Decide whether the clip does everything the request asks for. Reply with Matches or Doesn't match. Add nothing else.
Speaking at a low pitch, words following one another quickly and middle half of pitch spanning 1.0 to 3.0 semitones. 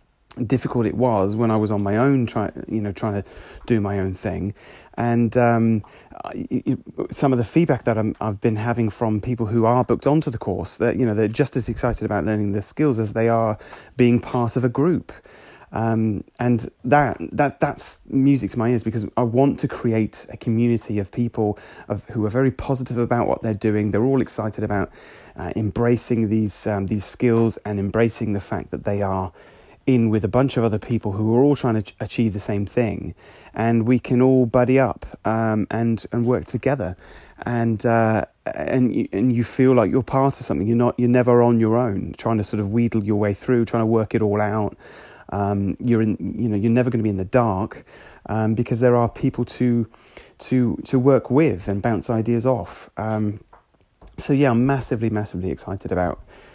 Matches